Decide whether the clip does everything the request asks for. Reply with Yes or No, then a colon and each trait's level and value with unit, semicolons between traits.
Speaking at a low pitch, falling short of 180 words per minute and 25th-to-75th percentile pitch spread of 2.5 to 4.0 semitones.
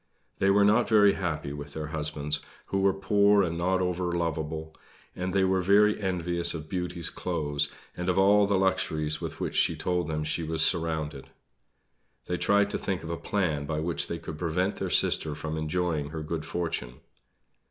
No: very low, 85 Hz; average, 185 wpm; average, 3.5 semitones